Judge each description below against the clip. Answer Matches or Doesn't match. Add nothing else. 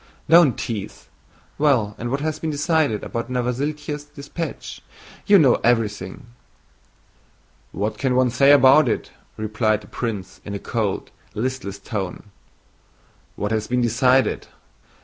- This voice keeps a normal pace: Doesn't match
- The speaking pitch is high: Doesn't match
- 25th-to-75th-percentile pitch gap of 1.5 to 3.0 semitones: Doesn't match